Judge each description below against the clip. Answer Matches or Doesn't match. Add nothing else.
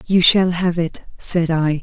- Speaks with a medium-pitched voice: Matches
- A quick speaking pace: Doesn't match